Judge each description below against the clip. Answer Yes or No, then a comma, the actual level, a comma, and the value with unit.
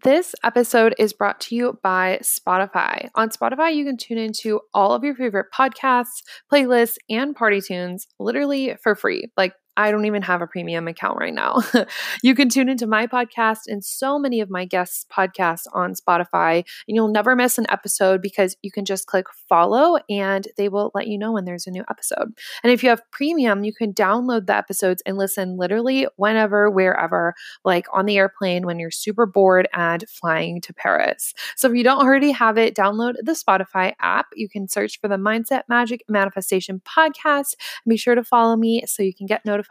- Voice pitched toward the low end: No, high, 215 Hz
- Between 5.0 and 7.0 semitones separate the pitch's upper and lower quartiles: No, average, 4.3 semitones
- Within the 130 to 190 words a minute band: No, average, 200 wpm